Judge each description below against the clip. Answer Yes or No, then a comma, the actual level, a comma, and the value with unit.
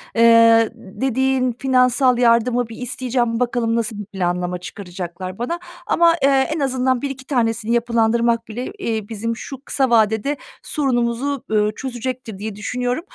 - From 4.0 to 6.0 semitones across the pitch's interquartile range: No, narrow, 2.6 semitones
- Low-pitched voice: No, high, 235 Hz